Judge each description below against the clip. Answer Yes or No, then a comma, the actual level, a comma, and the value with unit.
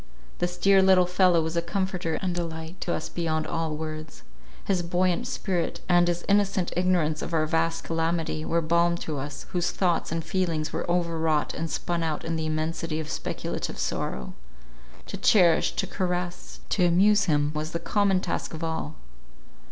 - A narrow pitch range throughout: Yes, narrow, 2.1 semitones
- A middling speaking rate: Yes, average, 175 wpm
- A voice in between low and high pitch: Yes, medium, 170 Hz